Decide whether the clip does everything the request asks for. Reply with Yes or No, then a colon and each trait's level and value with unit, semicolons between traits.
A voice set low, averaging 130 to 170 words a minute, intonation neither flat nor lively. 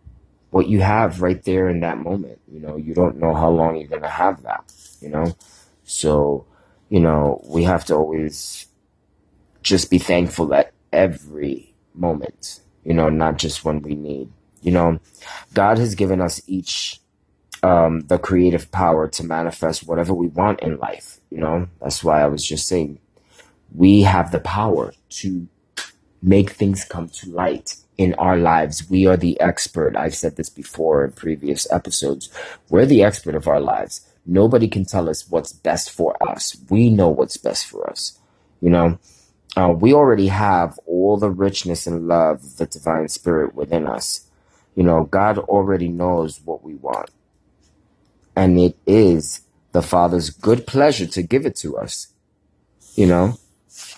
Yes: very low, 85 Hz; average, 165 wpm; average, 3.4 semitones